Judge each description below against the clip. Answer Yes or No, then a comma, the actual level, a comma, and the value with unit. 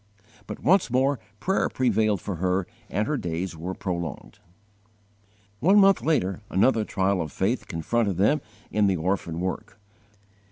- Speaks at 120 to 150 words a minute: Yes, average, 145 wpm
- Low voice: Yes, low, 100 Hz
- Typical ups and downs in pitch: No, wide, 5.9 semitones